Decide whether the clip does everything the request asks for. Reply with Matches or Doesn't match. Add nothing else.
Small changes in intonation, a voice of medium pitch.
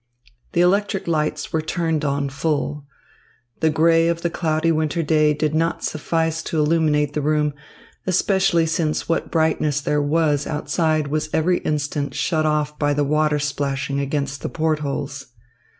Matches